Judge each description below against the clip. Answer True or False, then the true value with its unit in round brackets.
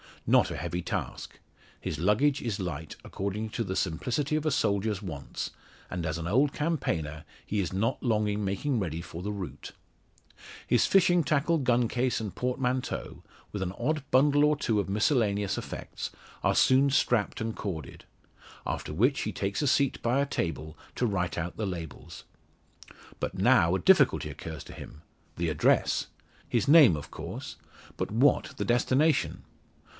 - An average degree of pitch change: False (6.8 semitones)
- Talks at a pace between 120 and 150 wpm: False (165 wpm)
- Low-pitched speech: True (110 Hz)